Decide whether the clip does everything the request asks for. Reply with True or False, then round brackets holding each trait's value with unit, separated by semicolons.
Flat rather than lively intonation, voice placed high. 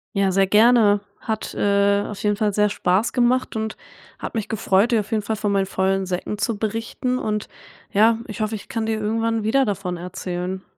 True (2.1 semitones; 210 Hz)